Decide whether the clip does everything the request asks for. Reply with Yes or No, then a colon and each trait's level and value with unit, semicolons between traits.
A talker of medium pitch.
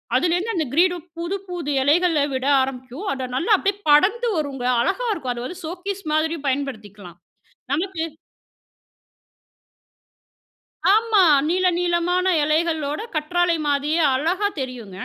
No: very high, 325 Hz